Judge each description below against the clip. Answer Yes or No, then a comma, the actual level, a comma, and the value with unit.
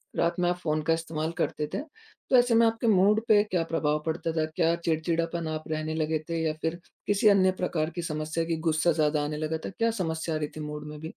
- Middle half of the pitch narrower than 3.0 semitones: Yes, narrow, 2.4 semitones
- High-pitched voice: No, medium, 165 Hz